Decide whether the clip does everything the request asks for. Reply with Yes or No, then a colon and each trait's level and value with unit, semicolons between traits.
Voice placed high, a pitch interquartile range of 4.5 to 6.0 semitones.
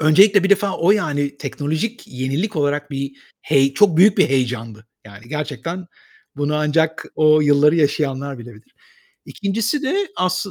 No: medium, 150 Hz; average, 5.3 semitones